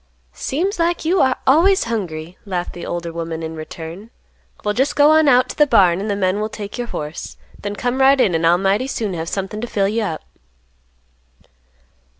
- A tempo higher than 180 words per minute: Yes, average, 200 wpm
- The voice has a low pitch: No, high, 205 Hz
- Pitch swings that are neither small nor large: No, wide, 7.1 semitones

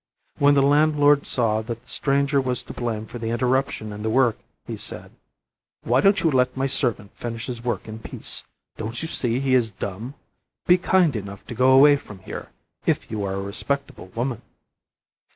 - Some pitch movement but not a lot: Yes, average, 3.9 semitones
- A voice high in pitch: No, low, 125 Hz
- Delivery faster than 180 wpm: Yes, average, 190 wpm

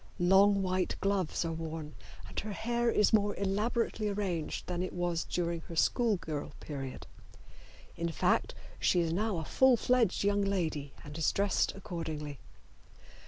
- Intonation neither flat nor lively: Yes, average, 3.9 semitones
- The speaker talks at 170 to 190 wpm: No, average, 155 wpm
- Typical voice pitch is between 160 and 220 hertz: Yes, medium, 185 Hz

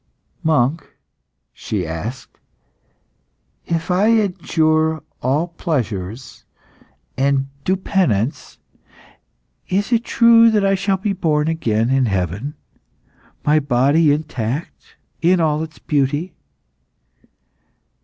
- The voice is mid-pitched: Yes, medium, 155 Hz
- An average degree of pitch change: No, wide, 5.7 semitones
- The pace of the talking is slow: Yes, slow, 95 wpm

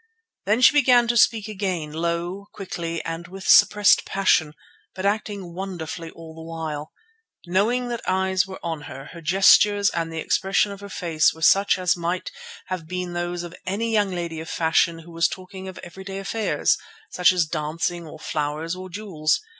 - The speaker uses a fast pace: No, average, 180 wpm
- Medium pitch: Yes, medium, 180 Hz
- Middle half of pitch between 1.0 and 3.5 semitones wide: Yes, average, 3.0 semitones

